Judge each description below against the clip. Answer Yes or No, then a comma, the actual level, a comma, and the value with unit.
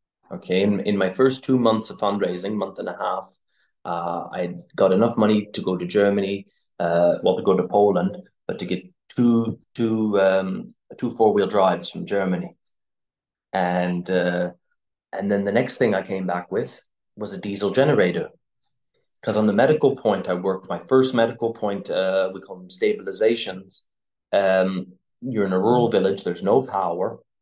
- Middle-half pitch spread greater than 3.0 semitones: Yes, average, 3.4 semitones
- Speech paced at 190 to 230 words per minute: No, average, 175 wpm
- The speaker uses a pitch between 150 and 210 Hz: No, very low, 95 Hz